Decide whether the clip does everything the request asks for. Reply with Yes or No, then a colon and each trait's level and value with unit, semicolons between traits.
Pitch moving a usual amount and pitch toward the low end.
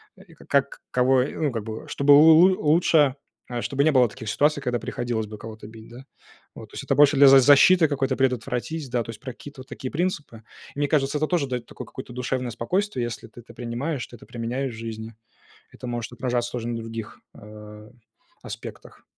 Yes: average, 3.6 semitones; low, 125 Hz